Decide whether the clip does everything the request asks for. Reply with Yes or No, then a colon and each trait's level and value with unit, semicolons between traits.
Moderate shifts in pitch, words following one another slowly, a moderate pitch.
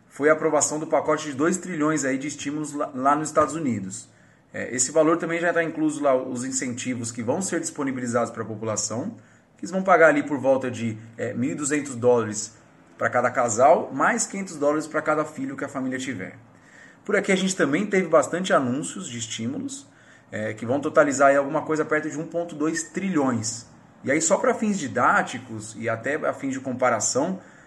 No: average, 4.4 semitones; fast, 185 wpm; medium, 150 Hz